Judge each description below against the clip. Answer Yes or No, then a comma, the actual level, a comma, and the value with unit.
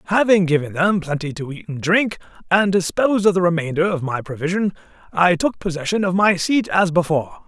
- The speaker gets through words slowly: No, average, 195 wpm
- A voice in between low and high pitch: Yes, medium, 175 Hz